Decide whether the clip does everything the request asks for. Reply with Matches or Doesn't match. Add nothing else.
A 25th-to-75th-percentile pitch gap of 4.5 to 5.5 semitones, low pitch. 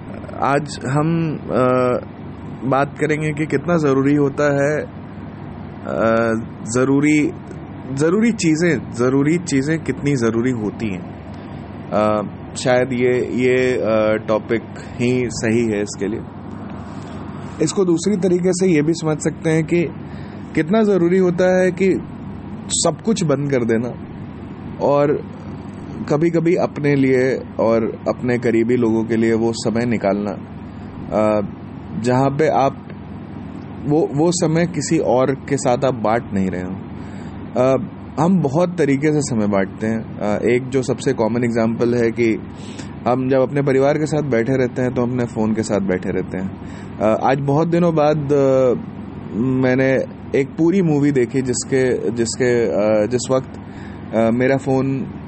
Matches